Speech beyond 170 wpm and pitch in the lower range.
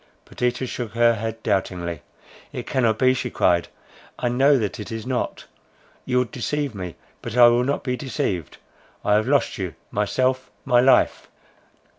No: average, 165 wpm; low, 120 Hz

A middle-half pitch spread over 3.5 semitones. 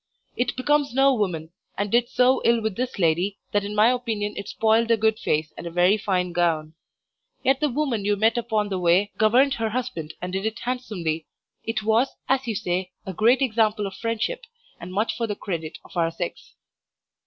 Yes: average, 4.6 semitones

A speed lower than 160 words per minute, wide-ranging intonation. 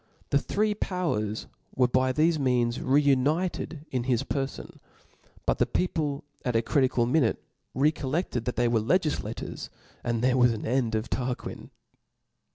No: average, 150 wpm; average, 3.9 semitones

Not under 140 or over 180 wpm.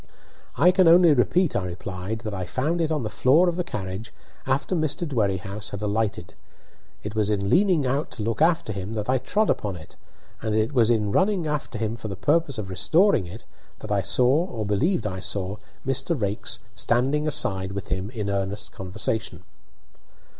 No: average, 190 wpm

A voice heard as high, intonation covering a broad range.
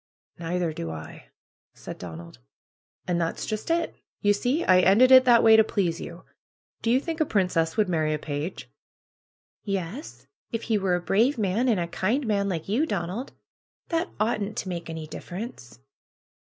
Yes: high, 195 Hz; wide, 5.7 semitones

